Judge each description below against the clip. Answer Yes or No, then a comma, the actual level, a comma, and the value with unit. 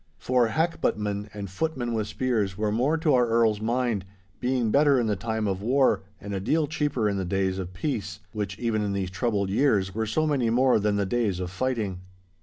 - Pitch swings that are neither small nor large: Yes, average, 4.2 semitones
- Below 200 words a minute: No, fast, 205 wpm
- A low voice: Yes, low, 110 Hz